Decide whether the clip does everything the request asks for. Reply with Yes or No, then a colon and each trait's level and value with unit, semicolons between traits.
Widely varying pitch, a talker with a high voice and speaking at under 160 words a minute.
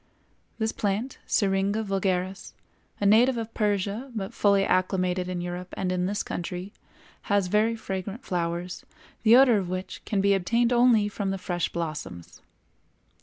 No: average, 3.0 semitones; high, 195 Hz; average, 150 wpm